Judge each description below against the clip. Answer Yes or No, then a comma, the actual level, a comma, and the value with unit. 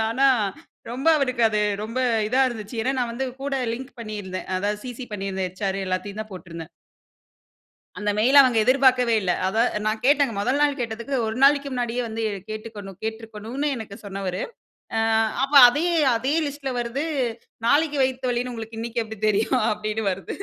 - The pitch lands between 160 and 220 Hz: No, high, 230 Hz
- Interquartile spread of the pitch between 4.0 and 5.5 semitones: No, average, 3.6 semitones